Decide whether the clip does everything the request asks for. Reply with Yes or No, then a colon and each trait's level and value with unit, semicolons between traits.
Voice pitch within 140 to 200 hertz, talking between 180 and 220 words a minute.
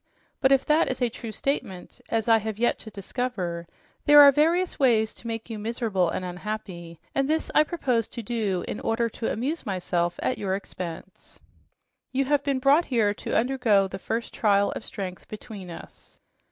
No: high, 225 Hz; average, 185 wpm